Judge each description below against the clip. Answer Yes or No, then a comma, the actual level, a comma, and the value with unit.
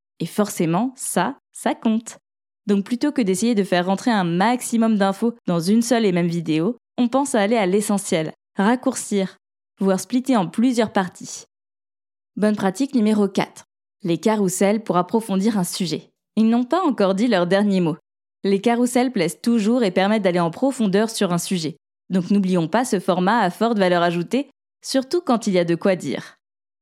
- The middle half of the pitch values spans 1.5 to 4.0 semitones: No, average, 4.5 semitones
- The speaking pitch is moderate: No, high, 200 Hz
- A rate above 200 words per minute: No, average, 180 wpm